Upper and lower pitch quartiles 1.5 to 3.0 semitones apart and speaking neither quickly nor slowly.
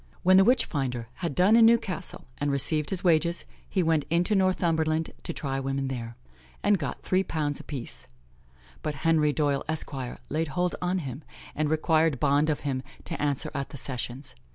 No: average, 4.1 semitones; average, 180 wpm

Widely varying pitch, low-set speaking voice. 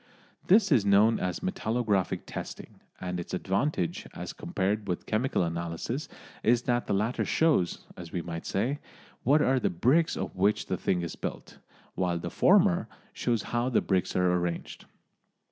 Yes: wide, 6.1 semitones; low, 105 Hz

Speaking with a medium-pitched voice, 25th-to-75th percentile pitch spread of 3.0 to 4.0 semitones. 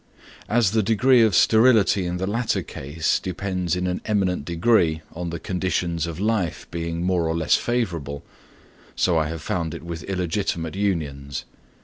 No: very low, 90 Hz; average, 3.6 semitones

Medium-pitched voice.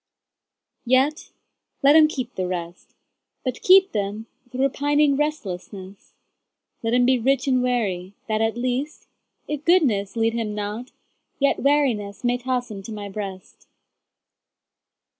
No: high, 245 Hz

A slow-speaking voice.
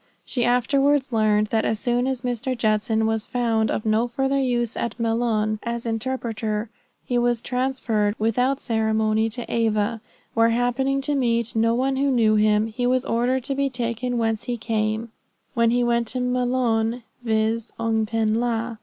No: average, 170 wpm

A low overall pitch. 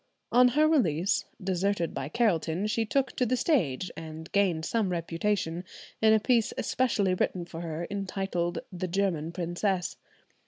No: medium, 185 Hz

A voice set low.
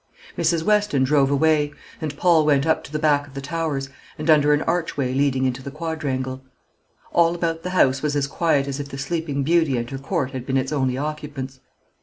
No: medium, 145 Hz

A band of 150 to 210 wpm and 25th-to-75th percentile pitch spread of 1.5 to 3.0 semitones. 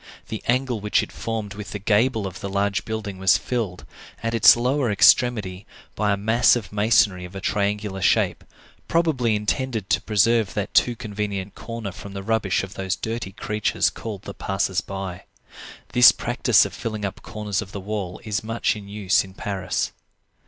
Yes: average, 180 wpm; narrow, 2.6 semitones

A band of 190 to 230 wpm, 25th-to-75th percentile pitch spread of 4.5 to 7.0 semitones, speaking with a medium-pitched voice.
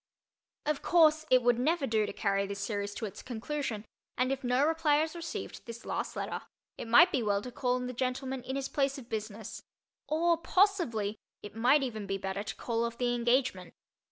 No: fast, 205 wpm; average, 4.8 semitones; very high, 250 Hz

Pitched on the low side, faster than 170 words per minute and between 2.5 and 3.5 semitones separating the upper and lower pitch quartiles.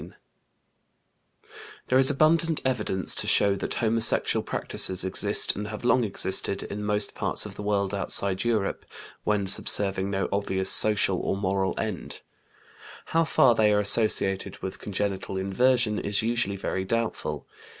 No: low, 105 Hz; average, 140 wpm; average, 2.9 semitones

